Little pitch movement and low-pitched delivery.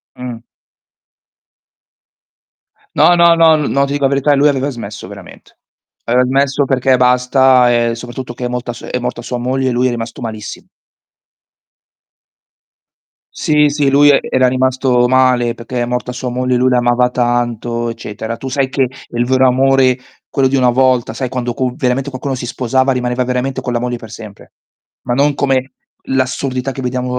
Yes: narrow, 1.6 semitones; low, 125 Hz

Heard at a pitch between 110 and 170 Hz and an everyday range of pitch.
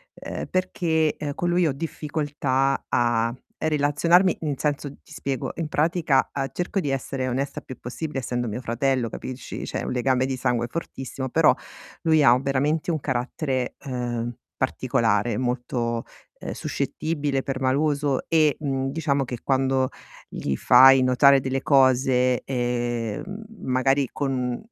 Yes: low, 135 Hz; average, 3.0 semitones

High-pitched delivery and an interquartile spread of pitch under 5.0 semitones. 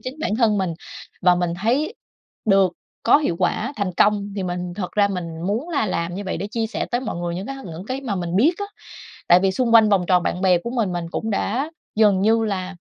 Yes: high, 200 Hz; average, 4.1 semitones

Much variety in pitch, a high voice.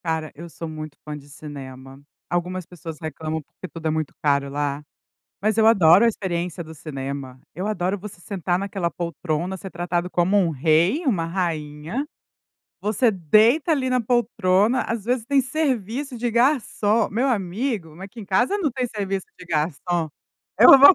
No: wide, 6.0 semitones; medium, 180 Hz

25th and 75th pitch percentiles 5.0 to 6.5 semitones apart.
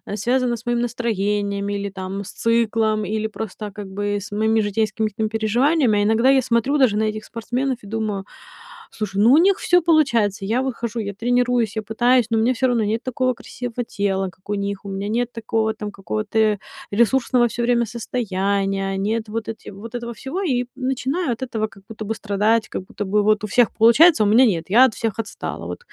No: average, 2.9 semitones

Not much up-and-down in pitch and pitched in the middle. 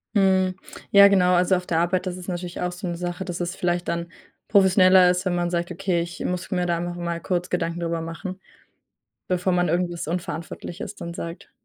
Yes: narrow, 1.2 semitones; medium, 180 Hz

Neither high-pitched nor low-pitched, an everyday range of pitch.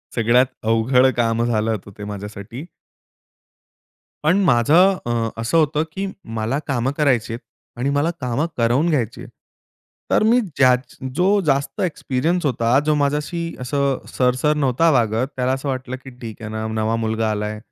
No: low, 125 Hz; average, 4.6 semitones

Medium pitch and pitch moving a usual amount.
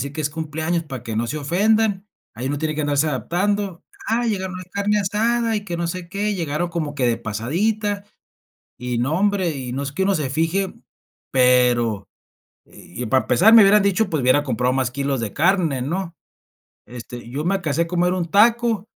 No: medium, 165 Hz; wide, 6.9 semitones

